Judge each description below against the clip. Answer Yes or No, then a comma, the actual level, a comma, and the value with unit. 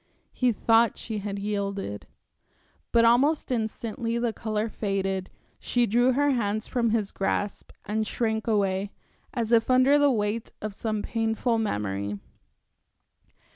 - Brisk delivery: No, slow, 135 wpm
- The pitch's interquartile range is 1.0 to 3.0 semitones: Yes, narrow, 2.6 semitones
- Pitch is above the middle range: Yes, high, 220 Hz